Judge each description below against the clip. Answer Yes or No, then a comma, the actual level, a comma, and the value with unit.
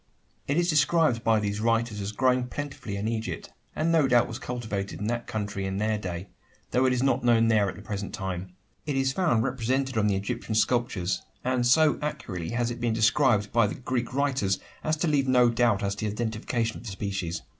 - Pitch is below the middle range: Yes, low, 115 Hz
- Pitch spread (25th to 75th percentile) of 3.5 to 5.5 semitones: Yes, average, 3.9 semitones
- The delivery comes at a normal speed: No, fast, 215 wpm